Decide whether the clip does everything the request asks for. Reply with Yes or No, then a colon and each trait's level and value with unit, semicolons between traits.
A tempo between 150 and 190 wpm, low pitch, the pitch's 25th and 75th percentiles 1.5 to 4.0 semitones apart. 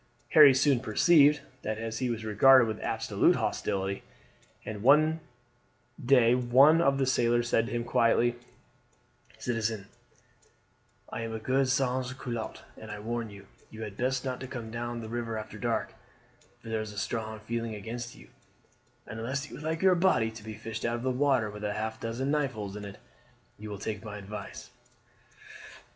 Yes: average, 180 wpm; low, 115 Hz; average, 3.0 semitones